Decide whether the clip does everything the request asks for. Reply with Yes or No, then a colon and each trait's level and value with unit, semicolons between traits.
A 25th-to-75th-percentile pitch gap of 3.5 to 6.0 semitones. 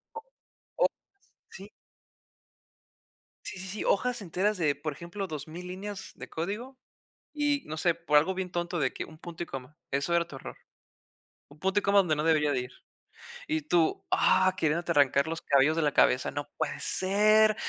Yes: average, 4.6 semitones